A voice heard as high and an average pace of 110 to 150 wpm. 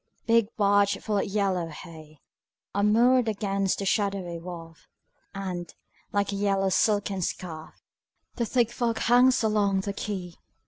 Yes: high, 200 Hz; average, 140 wpm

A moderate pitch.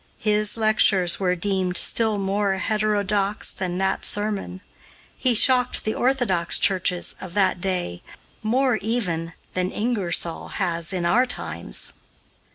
No: high, 195 Hz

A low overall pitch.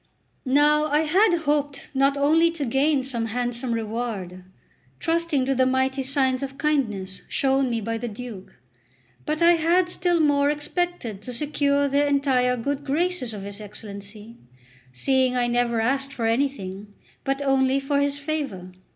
No: very high, 270 Hz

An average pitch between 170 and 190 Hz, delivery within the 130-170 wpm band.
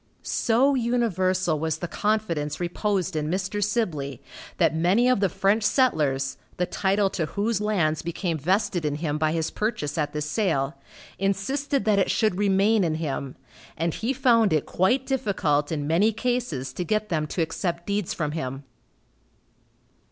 Yes: medium, 185 Hz; average, 160 wpm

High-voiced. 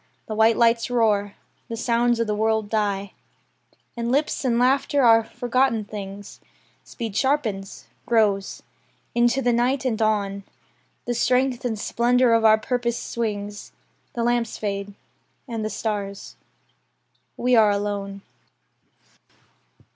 Yes: high, 225 Hz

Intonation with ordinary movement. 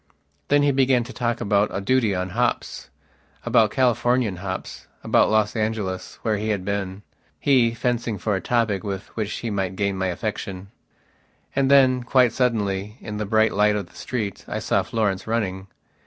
Yes: average, 3.5 semitones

